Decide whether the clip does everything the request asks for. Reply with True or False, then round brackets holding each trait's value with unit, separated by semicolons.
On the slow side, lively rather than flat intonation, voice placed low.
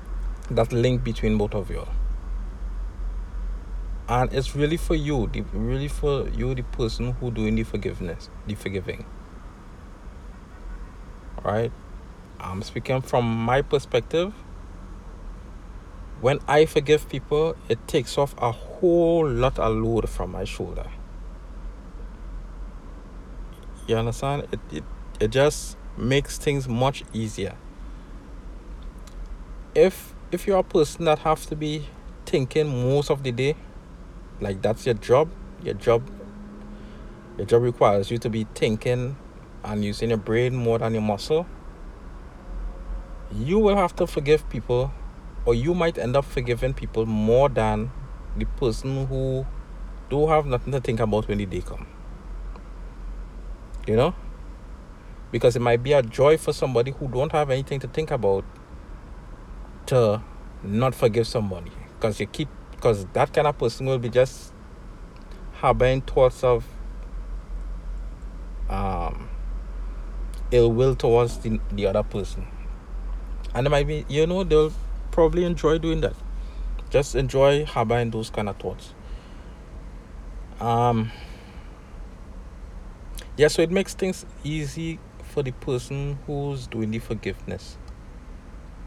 True (130 wpm; 6.7 semitones; 115 Hz)